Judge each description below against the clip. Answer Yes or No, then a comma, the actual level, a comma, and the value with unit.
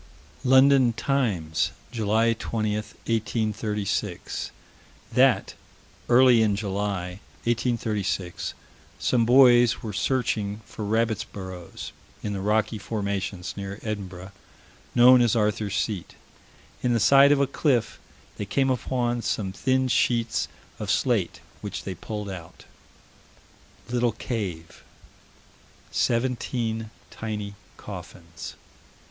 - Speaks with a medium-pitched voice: No, low, 110 Hz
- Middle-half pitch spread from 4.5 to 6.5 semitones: No, average, 3.2 semitones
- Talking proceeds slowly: Yes, slow, 105 wpm